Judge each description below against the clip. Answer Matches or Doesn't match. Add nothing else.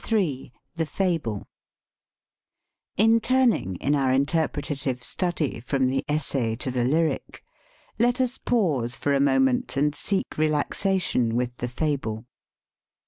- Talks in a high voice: Doesn't match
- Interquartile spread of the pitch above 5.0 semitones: Matches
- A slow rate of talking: Matches